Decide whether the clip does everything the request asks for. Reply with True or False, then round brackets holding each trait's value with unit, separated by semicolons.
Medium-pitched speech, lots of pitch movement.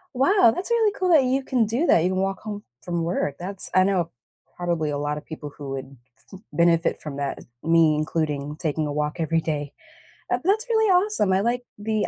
True (175 Hz; 7.9 semitones)